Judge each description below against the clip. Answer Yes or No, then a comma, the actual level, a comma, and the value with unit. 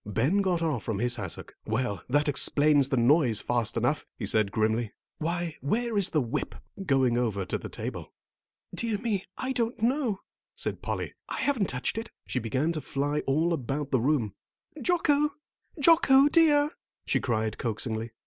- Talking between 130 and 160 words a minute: No, average, 170 wpm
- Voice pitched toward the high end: No, medium, 145 Hz